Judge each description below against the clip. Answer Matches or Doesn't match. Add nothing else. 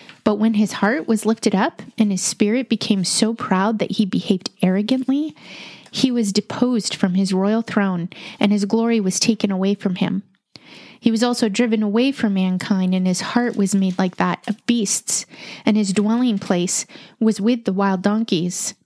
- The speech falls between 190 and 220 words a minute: Doesn't match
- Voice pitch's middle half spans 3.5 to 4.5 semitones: Doesn't match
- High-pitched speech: Matches